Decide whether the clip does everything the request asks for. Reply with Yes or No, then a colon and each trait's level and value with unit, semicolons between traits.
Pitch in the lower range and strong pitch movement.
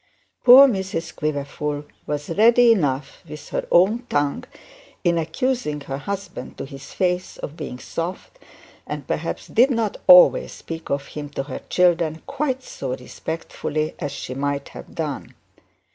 No: medium, 160 Hz; wide, 6.1 semitones